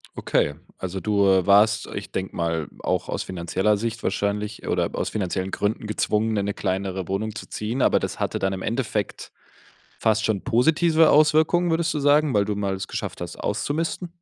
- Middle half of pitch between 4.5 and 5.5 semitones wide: Yes, average, 5.1 semitones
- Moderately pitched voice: No, low, 105 Hz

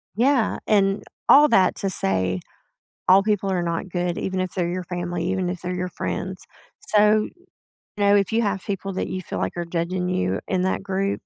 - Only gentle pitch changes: Yes, narrow, 2.2 semitones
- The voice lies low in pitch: No, medium, 185 Hz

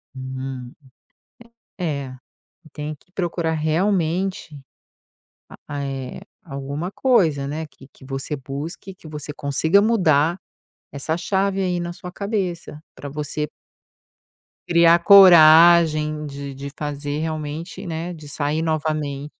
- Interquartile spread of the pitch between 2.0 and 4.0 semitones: Yes, average, 3.3 semitones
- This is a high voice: No, medium, 155 Hz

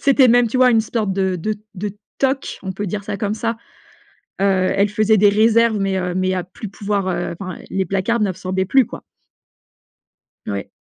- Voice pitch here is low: No, high, 200 Hz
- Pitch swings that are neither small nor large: Yes, average, 3.0 semitones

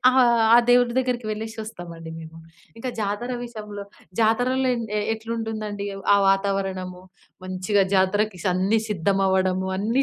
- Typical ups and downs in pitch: Yes, average, 3.1 semitones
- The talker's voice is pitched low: No, high, 205 Hz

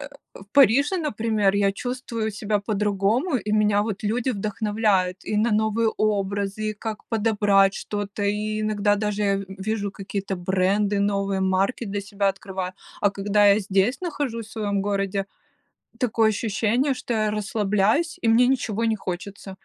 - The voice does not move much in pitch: Yes, narrow, 2.0 semitones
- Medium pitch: No, high, 210 Hz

